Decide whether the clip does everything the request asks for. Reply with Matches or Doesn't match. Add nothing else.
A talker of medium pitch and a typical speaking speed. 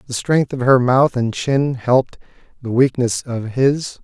Doesn't match